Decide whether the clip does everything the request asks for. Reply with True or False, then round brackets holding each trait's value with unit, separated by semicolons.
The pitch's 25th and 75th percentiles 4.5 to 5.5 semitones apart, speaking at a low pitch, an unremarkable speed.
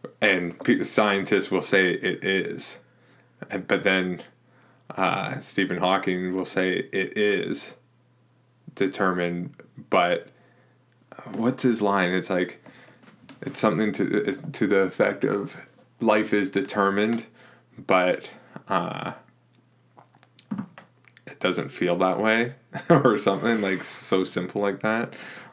False (4.8 semitones; 105 Hz; 115 wpm)